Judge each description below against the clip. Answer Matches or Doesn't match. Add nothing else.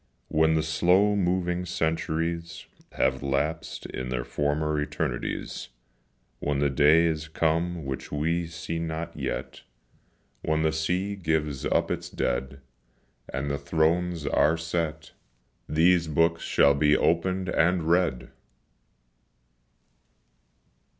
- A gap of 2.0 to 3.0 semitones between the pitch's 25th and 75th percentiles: Matches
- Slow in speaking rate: Matches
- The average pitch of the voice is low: Matches